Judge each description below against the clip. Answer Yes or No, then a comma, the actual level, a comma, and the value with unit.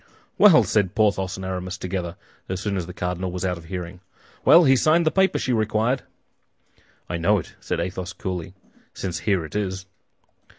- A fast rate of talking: No, average, 180 wpm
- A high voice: No, very low, 95 Hz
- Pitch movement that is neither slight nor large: Yes, average, 3.2 semitones